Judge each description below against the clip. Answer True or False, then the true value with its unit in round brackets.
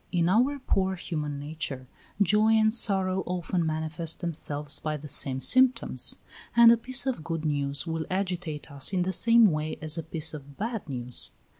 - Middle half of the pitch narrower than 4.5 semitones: False (5.2 semitones)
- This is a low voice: False (165 Hz)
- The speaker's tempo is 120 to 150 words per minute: False (175 wpm)